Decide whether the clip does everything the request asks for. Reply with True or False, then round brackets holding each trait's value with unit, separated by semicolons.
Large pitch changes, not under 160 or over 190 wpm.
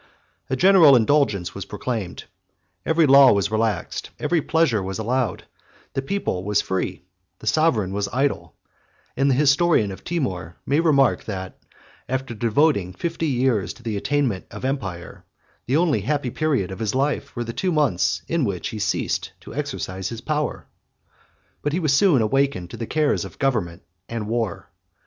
True (6.5 semitones; 165 wpm)